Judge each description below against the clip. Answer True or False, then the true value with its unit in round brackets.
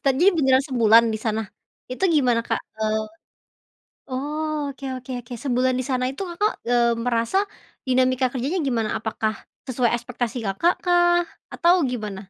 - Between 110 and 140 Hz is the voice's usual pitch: False (255 Hz)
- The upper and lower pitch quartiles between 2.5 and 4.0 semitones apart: True (3.1 semitones)